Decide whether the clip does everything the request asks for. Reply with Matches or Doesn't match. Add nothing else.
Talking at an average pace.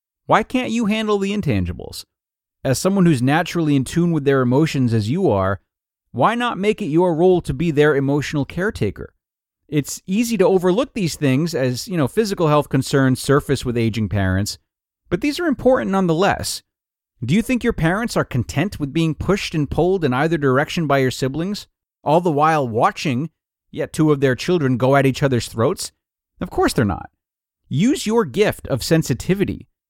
Matches